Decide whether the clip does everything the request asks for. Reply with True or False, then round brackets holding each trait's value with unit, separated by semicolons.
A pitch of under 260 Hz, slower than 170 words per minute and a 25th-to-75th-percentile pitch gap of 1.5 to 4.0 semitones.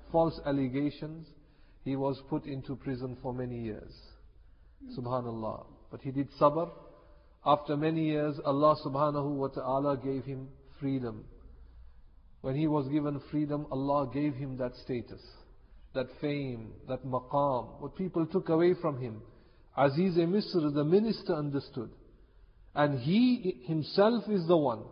True (140 Hz; 140 wpm; 3.3 semitones)